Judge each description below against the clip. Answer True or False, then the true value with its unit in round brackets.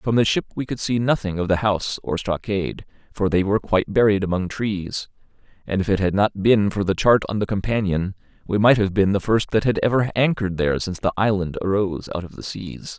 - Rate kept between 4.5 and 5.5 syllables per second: False (5.9 syllables/s)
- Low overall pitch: True (100 Hz)